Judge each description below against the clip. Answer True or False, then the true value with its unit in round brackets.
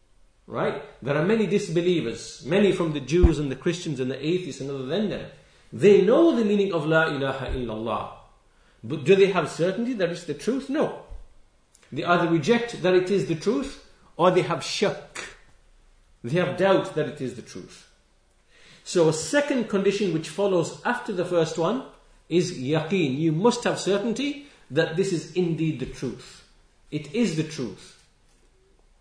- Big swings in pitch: False (4.9 semitones)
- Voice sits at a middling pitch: True (170 Hz)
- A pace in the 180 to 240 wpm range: False (170 wpm)